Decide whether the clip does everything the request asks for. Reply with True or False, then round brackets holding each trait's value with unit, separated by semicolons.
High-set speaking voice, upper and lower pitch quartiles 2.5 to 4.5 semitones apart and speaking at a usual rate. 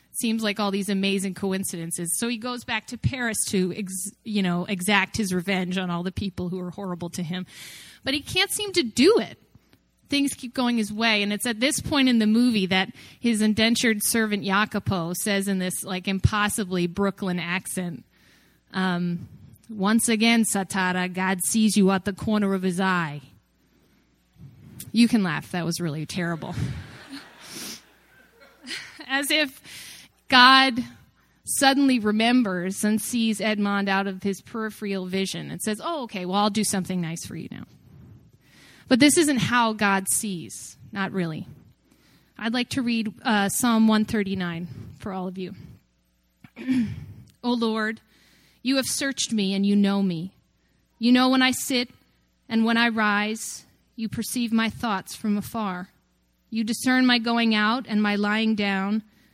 True (205 Hz; 3.7 semitones; 160 wpm)